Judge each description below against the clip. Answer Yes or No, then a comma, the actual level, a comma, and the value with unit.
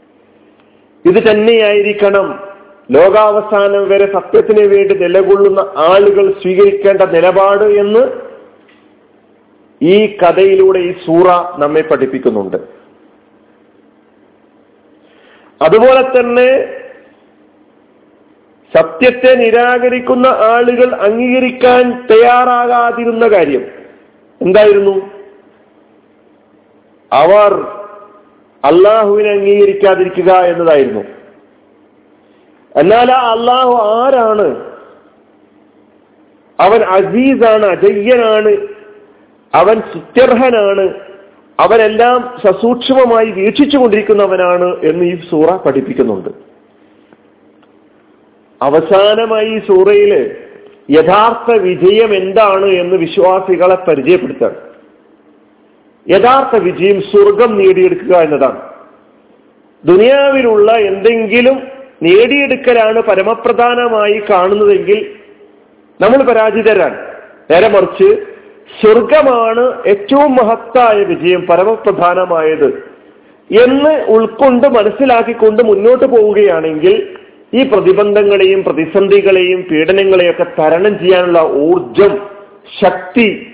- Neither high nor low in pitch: No, high, 220 Hz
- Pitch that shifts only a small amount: No, average, 4.7 semitones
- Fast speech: No, average, 65 wpm